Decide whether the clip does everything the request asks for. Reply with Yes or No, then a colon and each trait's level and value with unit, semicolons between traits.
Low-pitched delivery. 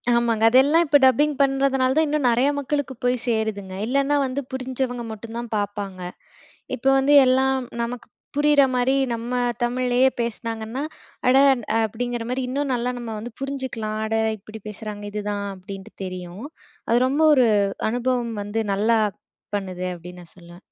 No: high, 240 Hz